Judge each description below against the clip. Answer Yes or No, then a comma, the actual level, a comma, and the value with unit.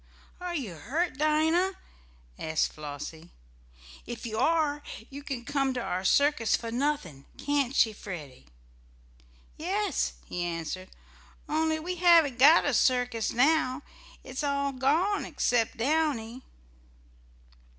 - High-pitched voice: Yes, very high, 270 Hz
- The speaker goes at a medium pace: No, slow, 120 wpm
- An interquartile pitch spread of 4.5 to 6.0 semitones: Yes, wide, 5.6 semitones